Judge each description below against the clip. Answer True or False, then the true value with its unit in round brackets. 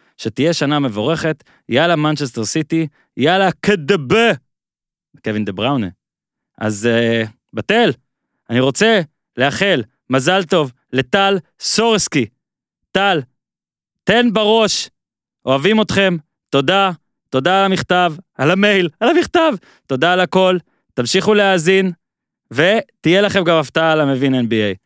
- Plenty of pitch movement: True (6.3 semitones)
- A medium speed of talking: True (110 wpm)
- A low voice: False (170 Hz)